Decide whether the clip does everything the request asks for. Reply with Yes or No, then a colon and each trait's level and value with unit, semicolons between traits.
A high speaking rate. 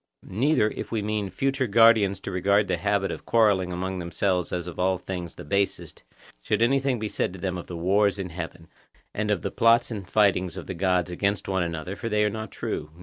Yes: fast, 230 wpm